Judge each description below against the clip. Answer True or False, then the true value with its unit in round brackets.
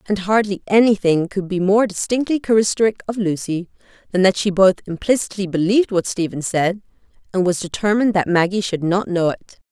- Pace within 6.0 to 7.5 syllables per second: True (6.1 syllables/s)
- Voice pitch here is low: False (195 Hz)